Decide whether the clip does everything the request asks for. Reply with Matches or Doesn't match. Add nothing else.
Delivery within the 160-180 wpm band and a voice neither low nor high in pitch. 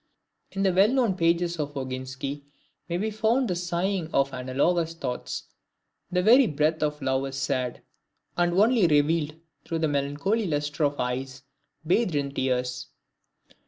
Doesn't match